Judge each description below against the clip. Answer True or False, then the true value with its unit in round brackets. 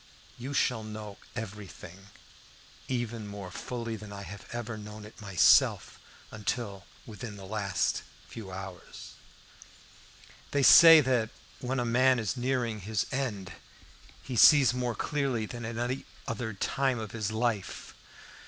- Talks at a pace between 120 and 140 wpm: True (135 wpm)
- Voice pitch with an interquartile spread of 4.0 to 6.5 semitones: False (3.2 semitones)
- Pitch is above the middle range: False (110 Hz)